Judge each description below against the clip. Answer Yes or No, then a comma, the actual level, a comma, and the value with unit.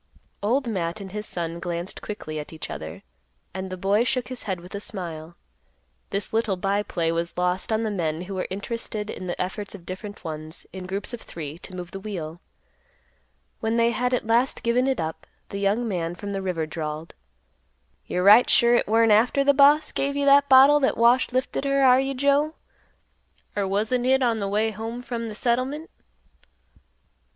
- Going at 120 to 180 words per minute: No, average, 195 wpm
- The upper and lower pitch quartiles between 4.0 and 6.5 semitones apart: Yes, average, 5.3 semitones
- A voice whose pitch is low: No, high, 210 Hz